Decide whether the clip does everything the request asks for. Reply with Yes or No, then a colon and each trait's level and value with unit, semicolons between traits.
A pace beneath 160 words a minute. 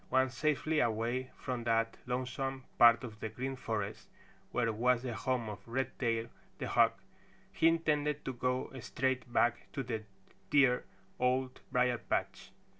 Yes: average, 145 wpm